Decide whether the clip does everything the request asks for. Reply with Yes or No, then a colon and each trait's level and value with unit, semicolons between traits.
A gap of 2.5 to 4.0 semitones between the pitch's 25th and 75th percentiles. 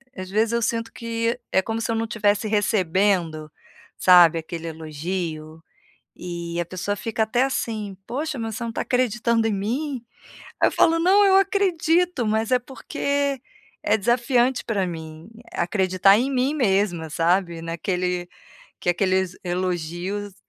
No: average, 5.2 semitones